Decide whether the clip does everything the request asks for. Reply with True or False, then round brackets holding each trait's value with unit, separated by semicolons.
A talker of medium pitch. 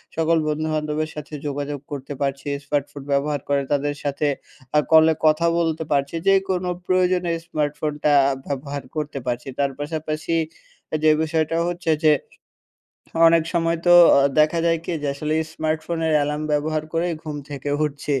True (155 Hz)